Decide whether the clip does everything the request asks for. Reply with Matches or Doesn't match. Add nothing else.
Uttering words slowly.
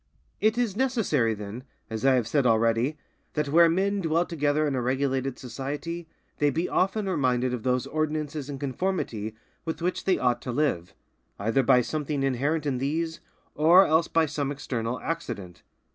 Doesn't match